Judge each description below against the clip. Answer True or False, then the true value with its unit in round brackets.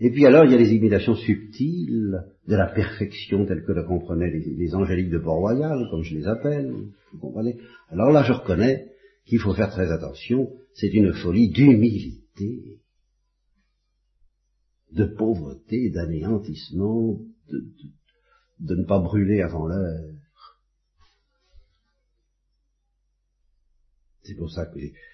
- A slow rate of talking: True (135 wpm)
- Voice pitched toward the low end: True (100 Hz)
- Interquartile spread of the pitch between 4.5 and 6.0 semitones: True (5.2 semitones)